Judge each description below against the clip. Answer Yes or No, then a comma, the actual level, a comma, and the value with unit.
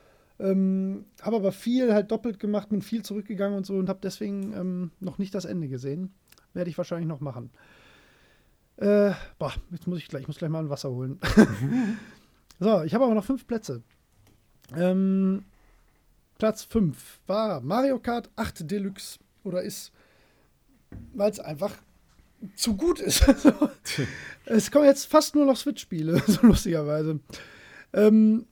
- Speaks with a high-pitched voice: Yes, high, 200 Hz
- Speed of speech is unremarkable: Yes, average, 150 wpm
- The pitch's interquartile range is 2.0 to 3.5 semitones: No, average, 4.1 semitones